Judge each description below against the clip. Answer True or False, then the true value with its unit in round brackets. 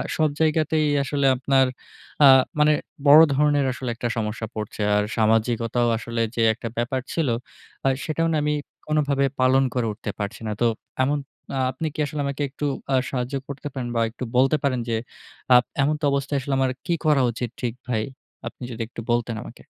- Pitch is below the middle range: True (130 Hz)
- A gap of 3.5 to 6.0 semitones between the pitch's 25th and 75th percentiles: True (3.9 semitones)